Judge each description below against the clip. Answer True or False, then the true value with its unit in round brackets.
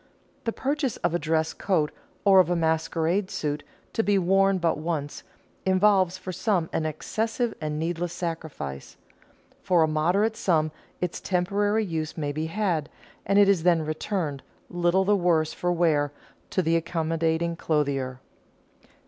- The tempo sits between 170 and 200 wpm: False (150 wpm)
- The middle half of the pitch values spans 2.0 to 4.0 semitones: True (3.4 semitones)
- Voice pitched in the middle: True (170 Hz)